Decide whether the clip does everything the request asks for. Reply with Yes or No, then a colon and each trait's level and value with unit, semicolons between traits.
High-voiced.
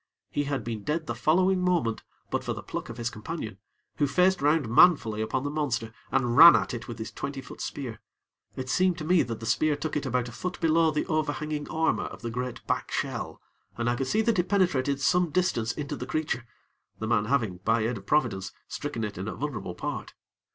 No: medium, 140 Hz